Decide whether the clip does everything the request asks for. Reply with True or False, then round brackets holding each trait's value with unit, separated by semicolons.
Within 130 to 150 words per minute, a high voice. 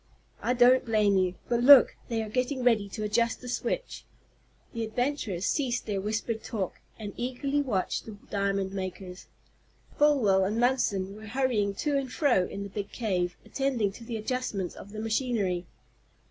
False (165 wpm; 220 Hz)